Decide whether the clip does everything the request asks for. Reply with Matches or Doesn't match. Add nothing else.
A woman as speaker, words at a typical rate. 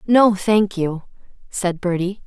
Doesn't match